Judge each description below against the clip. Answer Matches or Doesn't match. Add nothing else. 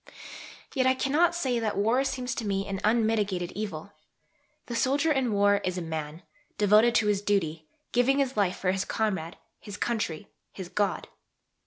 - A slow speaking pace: Doesn't match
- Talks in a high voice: Matches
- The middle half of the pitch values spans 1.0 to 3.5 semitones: Doesn't match